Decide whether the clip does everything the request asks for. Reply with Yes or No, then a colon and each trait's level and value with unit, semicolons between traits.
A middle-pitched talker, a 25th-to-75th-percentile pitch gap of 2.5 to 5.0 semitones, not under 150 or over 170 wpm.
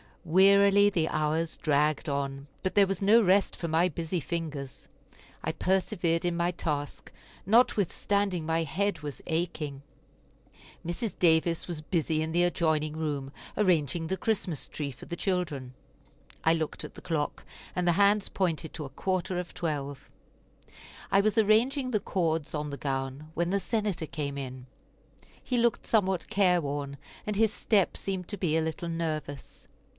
Yes: medium, 170 Hz; average, 4.2 semitones; average, 160 wpm